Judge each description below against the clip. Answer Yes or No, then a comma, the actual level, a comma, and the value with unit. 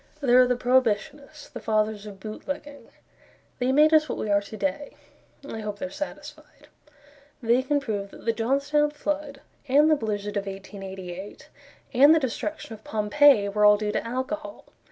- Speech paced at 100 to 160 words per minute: No, average, 170 wpm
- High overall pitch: Yes, high, 240 Hz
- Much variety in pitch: Yes, wide, 5.7 semitones